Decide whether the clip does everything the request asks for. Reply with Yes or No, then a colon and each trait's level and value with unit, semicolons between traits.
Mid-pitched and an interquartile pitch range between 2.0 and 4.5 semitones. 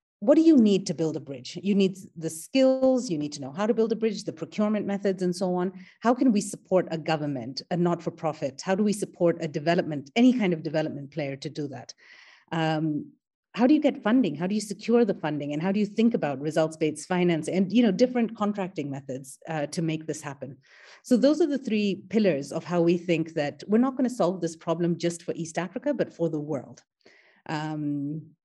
No: medium, 175 Hz; average, 5.3 semitones